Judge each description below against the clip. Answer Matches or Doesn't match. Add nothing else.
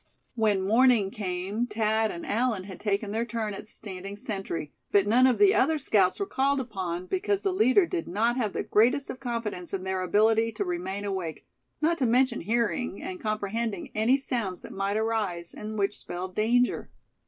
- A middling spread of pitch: Matches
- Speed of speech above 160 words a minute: Matches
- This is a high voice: Matches